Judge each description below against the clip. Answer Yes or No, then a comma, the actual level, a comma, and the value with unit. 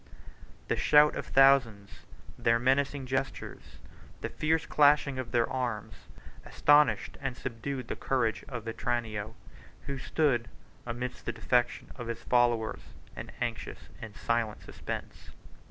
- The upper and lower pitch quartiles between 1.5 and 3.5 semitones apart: Yes, average, 2.9 semitones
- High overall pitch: No, low, 125 Hz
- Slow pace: Yes, slow, 125 wpm